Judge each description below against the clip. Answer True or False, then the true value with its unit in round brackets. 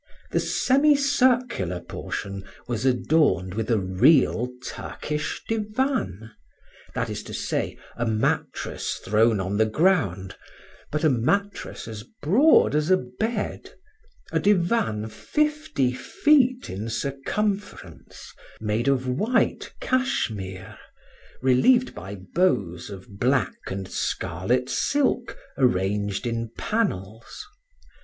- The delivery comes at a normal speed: False (105 wpm)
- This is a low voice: True (125 Hz)